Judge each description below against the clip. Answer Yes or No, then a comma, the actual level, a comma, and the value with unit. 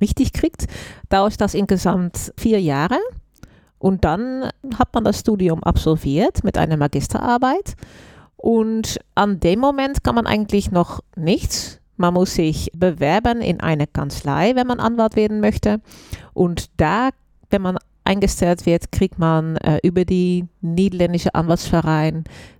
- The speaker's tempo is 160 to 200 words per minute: No, average, 135 wpm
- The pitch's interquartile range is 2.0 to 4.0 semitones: No, average, 5.1 semitones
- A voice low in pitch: No, medium, 185 Hz